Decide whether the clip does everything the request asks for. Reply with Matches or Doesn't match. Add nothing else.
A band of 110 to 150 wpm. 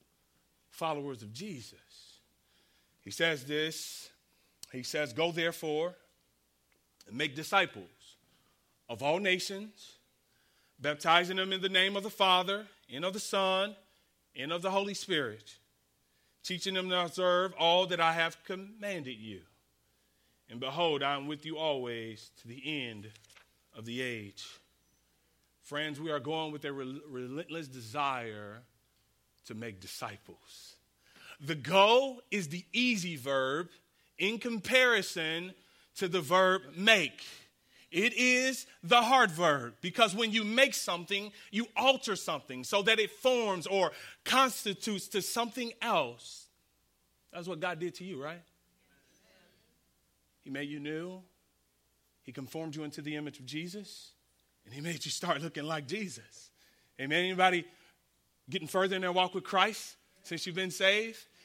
Matches